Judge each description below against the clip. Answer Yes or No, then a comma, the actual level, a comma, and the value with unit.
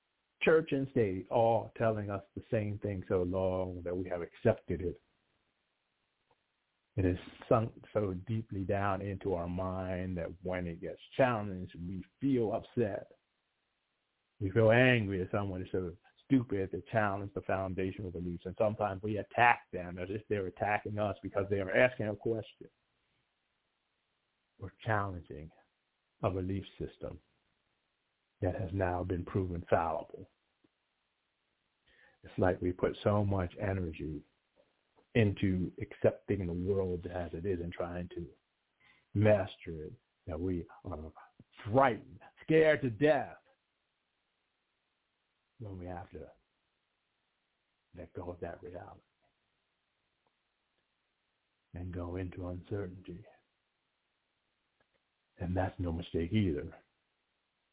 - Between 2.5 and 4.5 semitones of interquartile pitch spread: Yes, average, 2.8 semitones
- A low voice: Yes, very low, 95 Hz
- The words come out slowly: Yes, slow, 125 wpm